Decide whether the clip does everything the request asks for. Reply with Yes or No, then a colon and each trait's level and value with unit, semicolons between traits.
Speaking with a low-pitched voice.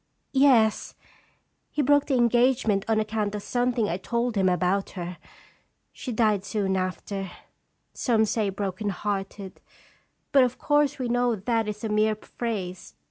No: high, 215 Hz